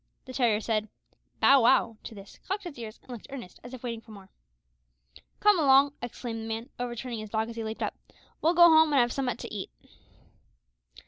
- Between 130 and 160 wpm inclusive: No, fast, 205 wpm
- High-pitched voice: Yes, high, 240 Hz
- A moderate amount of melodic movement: Yes, average, 3.7 semitones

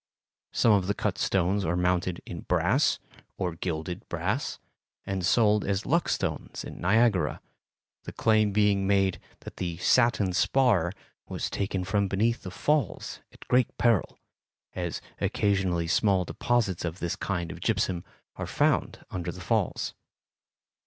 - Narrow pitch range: No, average, 3.1 semitones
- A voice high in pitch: No, very low, 95 Hz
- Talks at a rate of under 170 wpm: Yes, average, 145 wpm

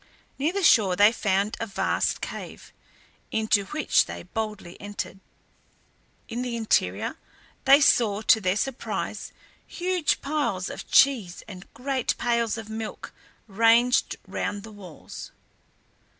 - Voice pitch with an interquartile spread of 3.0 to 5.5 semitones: Yes, average, 3.6 semitones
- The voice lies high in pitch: Yes, high, 225 Hz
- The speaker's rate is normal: No, slow, 125 wpm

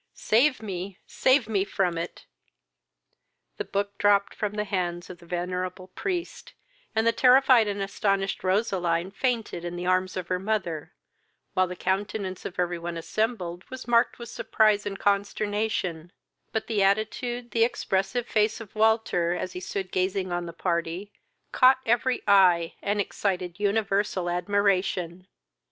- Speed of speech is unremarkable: Yes, average, 150 wpm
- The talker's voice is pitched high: Yes, high, 195 Hz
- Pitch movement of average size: Yes, average, 3.3 semitones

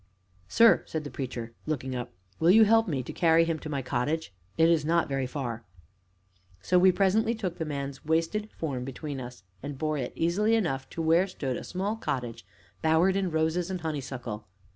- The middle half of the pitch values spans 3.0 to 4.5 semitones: No, average, 5.1 semitones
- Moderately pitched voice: Yes, medium, 160 Hz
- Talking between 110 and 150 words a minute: No, average, 190 wpm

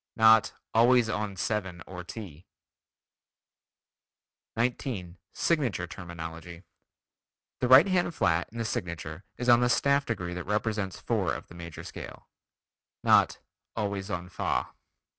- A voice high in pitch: No, low, 100 Hz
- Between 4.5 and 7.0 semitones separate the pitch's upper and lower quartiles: Yes, average, 5.3 semitones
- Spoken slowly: Yes, slow, 125 wpm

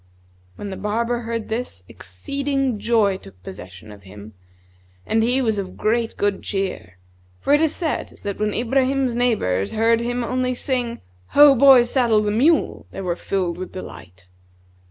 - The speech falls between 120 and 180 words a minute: Yes, average, 165 wpm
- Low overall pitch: No, high, 225 Hz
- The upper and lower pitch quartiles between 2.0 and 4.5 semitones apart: No, average, 5.1 semitones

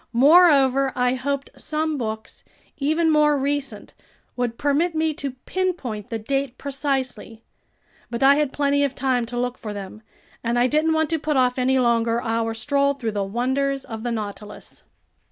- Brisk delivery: No, average, 170 wpm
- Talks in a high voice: Yes, very high, 265 Hz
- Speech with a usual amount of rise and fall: Yes, average, 3.6 semitones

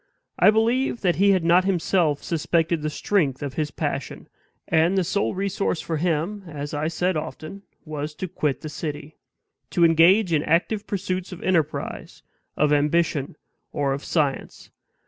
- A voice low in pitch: No, medium, 165 Hz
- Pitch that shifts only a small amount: No, average, 3.8 semitones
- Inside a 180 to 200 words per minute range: No, average, 160 wpm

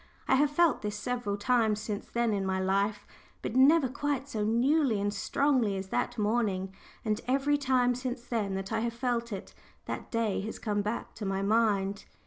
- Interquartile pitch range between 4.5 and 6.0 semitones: No, average, 3.7 semitones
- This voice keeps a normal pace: Yes, average, 190 wpm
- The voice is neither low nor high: No, high, 225 Hz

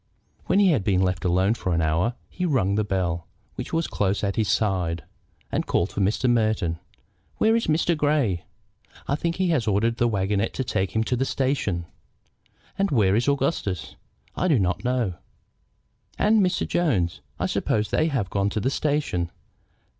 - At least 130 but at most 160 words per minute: No, average, 185 wpm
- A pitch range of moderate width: No, wide, 7.1 semitones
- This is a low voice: Yes, low, 110 Hz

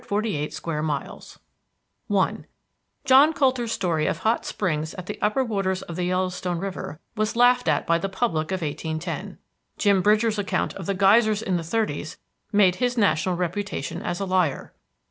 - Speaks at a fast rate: No, average, 170 wpm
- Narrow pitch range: No, average, 4.2 semitones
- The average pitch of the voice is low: No, high, 190 Hz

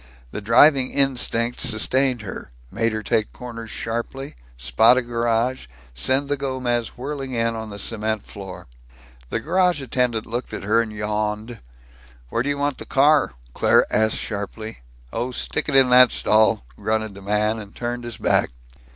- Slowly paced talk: No, average, 165 wpm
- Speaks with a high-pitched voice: No, low, 115 Hz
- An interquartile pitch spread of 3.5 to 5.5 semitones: No, average, 3.1 semitones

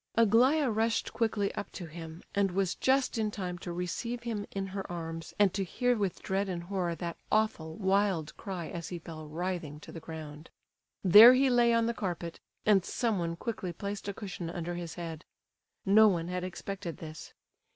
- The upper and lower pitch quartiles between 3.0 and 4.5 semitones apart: Yes, average, 4.0 semitones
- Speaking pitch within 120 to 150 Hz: No, high, 190 Hz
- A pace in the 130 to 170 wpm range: No, average, 185 wpm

